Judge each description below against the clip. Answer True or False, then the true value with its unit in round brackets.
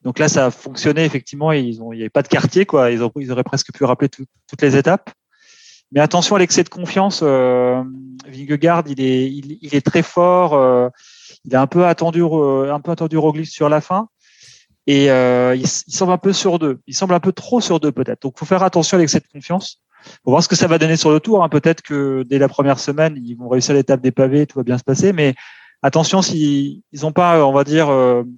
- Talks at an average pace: False (245 wpm)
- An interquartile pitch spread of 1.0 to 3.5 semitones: False (4.3 semitones)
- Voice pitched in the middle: True (150 Hz)